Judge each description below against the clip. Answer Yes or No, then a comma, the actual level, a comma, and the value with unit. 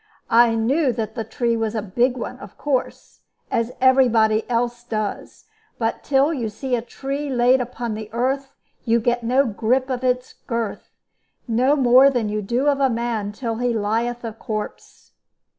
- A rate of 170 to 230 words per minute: Yes, average, 175 wpm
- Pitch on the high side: Yes, high, 240 Hz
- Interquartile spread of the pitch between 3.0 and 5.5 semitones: No, narrow, 2.5 semitones